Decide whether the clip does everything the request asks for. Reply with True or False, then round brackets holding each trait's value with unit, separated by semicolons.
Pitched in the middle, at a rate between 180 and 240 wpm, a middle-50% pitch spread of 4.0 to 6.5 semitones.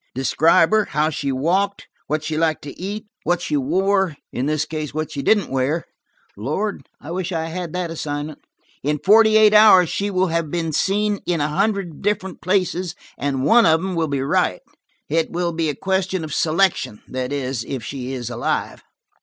True (165 Hz; 185 wpm; 4.5 semitones)